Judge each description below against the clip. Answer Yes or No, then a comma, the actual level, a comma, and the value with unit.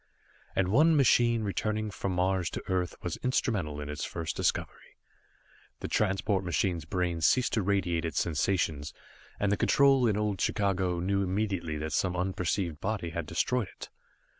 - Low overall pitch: Yes, very low, 95 Hz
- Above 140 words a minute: Yes, average, 160 wpm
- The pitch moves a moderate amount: Yes, average, 3.7 semitones